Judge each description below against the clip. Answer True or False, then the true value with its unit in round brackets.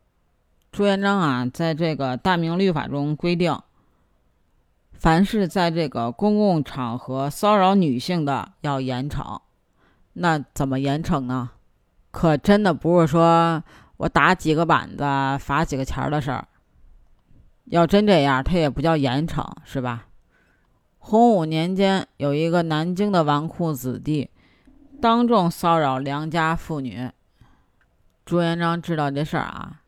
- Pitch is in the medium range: True (155 Hz)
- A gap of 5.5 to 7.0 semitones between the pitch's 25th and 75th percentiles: False (5.1 semitones)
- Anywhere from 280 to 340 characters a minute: False (200 characters per minute)